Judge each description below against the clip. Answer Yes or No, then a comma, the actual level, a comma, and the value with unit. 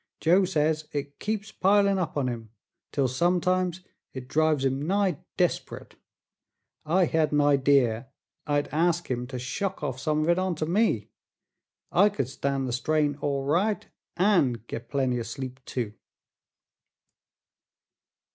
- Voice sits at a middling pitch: Yes, medium, 150 Hz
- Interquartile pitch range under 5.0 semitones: No, average, 5.3 semitones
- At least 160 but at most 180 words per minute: No, average, 140 wpm